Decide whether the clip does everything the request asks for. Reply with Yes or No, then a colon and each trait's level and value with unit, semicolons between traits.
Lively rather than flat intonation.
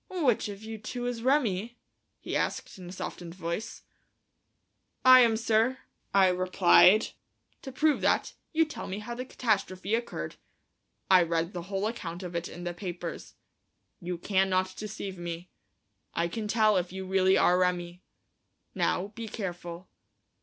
No: average, 4.0 semitones